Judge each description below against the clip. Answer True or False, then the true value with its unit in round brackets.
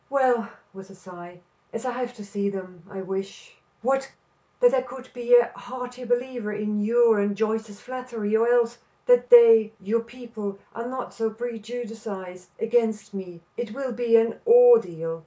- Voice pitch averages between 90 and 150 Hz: False (230 Hz)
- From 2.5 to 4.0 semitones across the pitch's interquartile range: True (3.2 semitones)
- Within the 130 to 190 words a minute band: True (170 wpm)